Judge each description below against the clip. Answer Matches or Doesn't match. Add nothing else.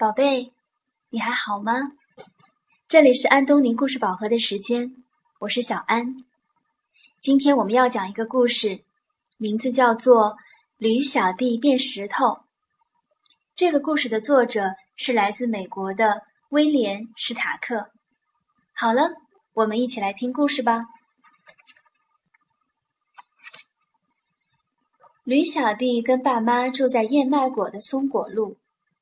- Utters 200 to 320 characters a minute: Doesn't match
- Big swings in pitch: Doesn't match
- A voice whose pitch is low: Doesn't match